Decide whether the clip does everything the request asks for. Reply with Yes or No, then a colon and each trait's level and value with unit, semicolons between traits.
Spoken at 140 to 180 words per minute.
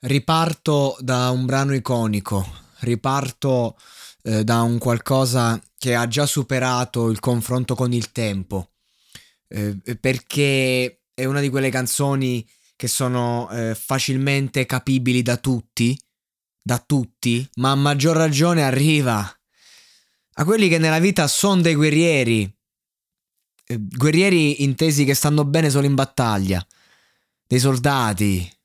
No: average, 125 wpm